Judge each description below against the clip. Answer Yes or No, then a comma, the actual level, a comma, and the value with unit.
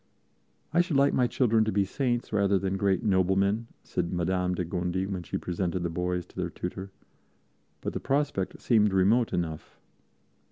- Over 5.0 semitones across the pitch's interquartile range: No, average, 3.8 semitones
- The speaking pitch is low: Yes, very low, 95 Hz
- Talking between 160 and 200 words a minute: Yes, average, 170 wpm